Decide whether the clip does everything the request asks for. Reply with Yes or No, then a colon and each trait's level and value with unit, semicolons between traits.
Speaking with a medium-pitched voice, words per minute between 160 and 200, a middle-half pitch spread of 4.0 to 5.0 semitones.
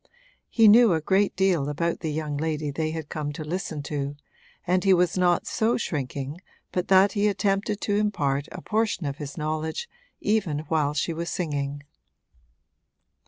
Yes: medium, 160 Hz; average, 165 wpm; average, 4.7 semitones